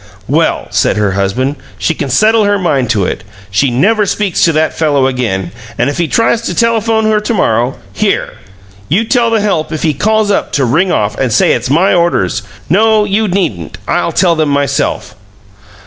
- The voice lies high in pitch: No, medium, 165 Hz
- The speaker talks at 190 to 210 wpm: Yes, average, 195 wpm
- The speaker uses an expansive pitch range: Yes, wide, 8.5 semitones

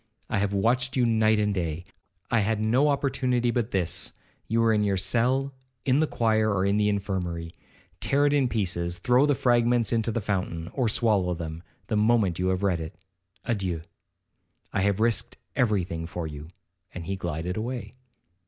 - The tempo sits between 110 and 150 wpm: No, average, 175 wpm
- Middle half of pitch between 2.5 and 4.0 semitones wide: No, average, 4.7 semitones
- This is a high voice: No, low, 105 Hz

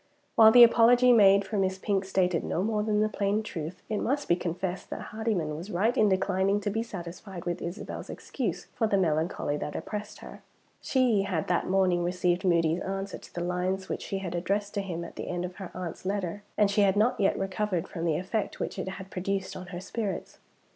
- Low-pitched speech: No, high, 190 Hz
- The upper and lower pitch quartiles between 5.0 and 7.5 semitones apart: No, average, 2.7 semitones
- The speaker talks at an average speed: No, fast, 215 wpm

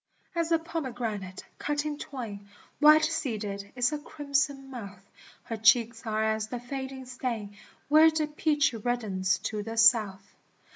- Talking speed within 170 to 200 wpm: No, average, 145 wpm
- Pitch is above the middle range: Yes, high, 245 Hz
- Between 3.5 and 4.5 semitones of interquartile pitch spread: No, wide, 5.4 semitones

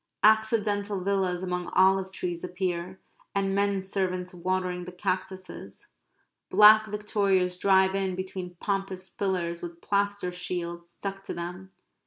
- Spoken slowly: Yes, slow, 125 wpm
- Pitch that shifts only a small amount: Yes, narrow, 1.8 semitones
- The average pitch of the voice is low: No, high, 190 Hz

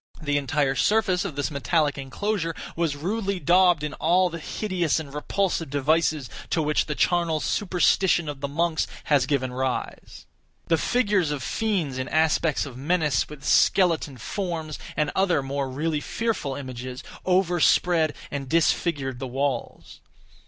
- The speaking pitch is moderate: Yes, medium, 155 Hz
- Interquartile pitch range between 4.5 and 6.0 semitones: No, average, 4.0 semitones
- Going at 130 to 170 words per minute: Yes, average, 145 wpm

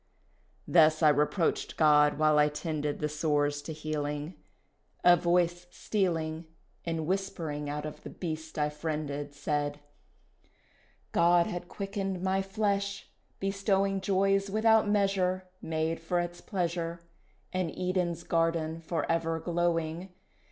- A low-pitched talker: No, medium, 165 Hz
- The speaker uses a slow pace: Yes, slow, 125 wpm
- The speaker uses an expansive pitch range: No, average, 3.3 semitones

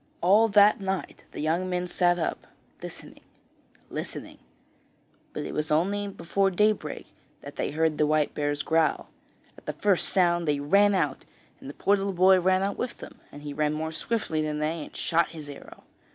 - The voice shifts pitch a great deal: No, average, 4.2 semitones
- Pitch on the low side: No, medium, 175 Hz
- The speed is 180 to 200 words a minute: Yes, average, 185 wpm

